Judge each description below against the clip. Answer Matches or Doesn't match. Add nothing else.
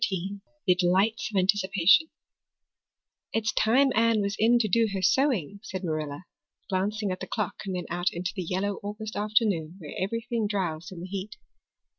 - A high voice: Matches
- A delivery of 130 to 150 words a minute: Doesn't match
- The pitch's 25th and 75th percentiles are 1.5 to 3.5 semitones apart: Matches